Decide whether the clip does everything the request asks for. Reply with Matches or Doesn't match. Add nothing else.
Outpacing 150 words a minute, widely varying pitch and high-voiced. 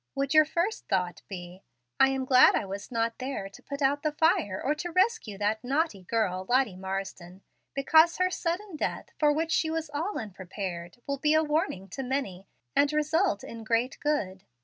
Matches